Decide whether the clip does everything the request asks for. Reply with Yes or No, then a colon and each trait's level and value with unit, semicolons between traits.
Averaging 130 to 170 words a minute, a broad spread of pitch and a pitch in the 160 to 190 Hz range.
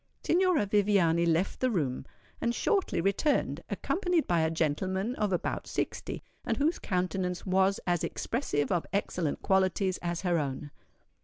No: average, 145 wpm; average, 3.7 semitones; medium, 185 Hz